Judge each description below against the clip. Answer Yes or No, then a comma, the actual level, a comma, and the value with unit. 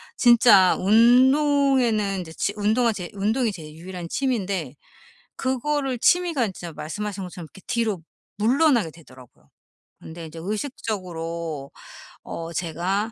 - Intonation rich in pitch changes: Yes, wide, 6.2 semitones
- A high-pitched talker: Yes, high, 205 Hz